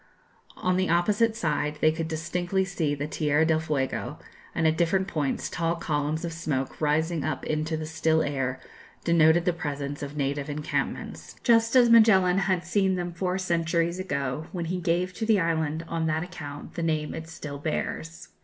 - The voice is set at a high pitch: No, medium, 165 Hz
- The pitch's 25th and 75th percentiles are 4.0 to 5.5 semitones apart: No, average, 2.9 semitones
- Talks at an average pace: Yes, average, 180 wpm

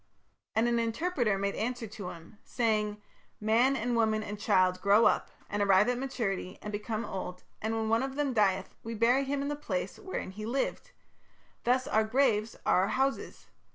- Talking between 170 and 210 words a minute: Yes, average, 190 wpm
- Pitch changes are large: No, average, 3.5 semitones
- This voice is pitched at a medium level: No, high, 220 Hz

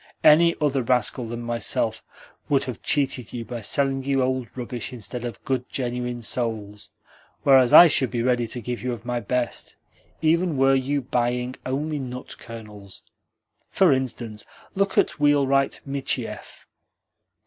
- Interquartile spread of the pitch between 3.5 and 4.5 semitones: No, narrow, 2.5 semitones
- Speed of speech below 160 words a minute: Yes, average, 150 wpm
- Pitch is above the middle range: No, low, 125 Hz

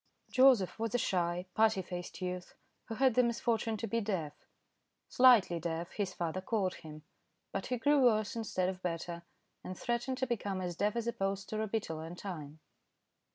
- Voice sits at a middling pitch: No, high, 195 Hz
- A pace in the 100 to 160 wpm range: No, average, 185 wpm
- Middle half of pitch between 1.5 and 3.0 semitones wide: No, average, 4.6 semitones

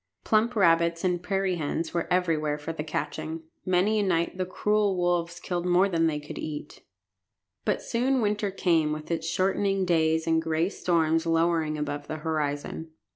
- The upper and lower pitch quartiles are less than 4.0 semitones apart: Yes, average, 2.7 semitones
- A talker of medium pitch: Yes, medium, 170 Hz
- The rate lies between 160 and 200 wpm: Yes, average, 170 wpm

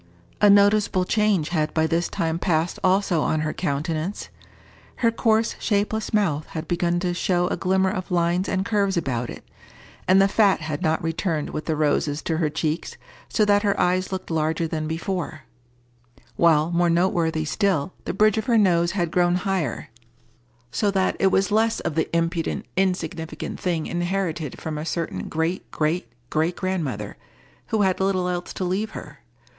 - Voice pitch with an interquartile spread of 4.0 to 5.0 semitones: No, average, 3.3 semitones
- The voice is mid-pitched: Yes, medium, 175 Hz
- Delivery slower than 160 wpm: No, average, 170 wpm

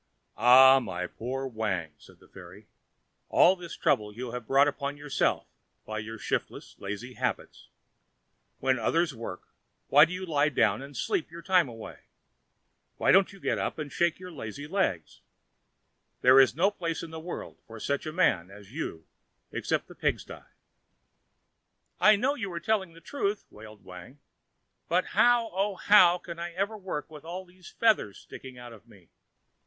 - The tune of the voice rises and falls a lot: Yes, wide, 8.0 semitones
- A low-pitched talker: No, medium, 145 Hz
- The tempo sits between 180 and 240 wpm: No, average, 170 wpm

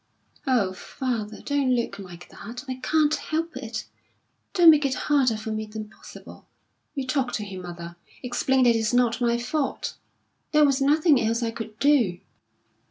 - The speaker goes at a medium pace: Yes, average, 165 wpm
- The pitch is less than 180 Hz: No, high, 245 Hz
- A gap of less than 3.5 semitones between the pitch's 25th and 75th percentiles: No, average, 4.2 semitones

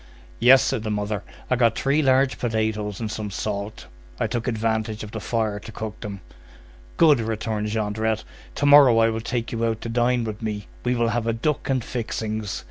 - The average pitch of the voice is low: Yes, low, 110 Hz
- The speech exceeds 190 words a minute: Yes, average, 200 wpm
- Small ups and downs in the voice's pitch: Yes, narrow, 2.0 semitones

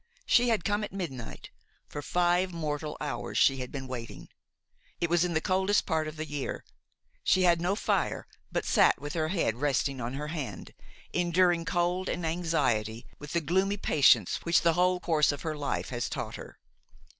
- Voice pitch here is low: No, medium, 165 Hz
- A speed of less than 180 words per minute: No, average, 185 wpm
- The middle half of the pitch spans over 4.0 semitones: No, average, 3.7 semitones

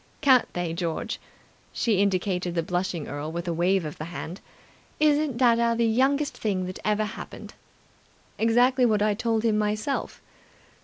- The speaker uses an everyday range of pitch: Yes, average, 4.8 semitones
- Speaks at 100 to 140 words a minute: No, average, 155 wpm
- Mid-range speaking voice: No, high, 210 Hz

